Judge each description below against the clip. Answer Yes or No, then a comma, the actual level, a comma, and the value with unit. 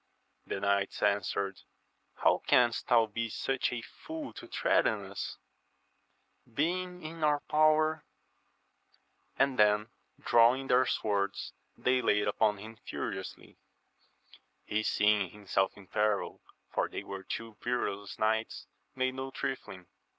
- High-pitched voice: No, low, 115 Hz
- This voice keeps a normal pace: No, slow, 120 wpm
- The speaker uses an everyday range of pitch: Yes, average, 4.5 semitones